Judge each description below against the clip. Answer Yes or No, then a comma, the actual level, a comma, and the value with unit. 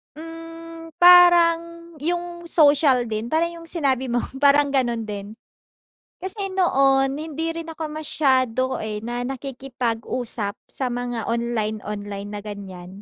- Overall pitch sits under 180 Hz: No, very high, 270 Hz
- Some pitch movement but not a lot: No, wide, 6.0 semitones